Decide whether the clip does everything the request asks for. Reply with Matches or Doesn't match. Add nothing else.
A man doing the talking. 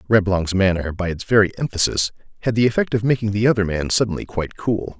Matches